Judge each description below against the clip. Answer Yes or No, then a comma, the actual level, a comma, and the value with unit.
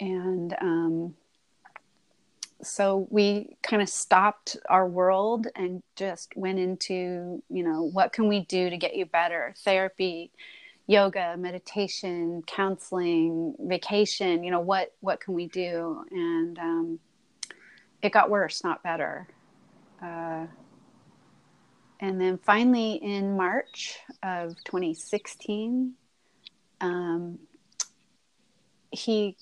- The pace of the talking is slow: Yes, slow, 110 wpm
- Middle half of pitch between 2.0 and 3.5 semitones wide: Yes, average, 2.9 semitones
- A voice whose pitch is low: No, high, 190 Hz